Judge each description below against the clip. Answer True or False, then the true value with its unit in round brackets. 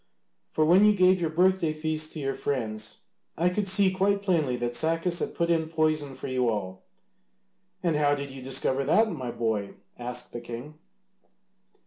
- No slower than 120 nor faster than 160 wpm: False (175 wpm)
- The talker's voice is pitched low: False (155 Hz)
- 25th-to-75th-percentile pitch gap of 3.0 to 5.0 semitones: False (5.6 semitones)